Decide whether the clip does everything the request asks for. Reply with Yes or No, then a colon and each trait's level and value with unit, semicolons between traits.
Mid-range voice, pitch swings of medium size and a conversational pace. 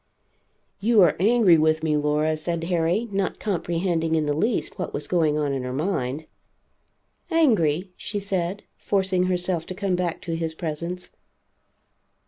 Yes: medium, 170 Hz; average, 3.3 semitones; average, 150 wpm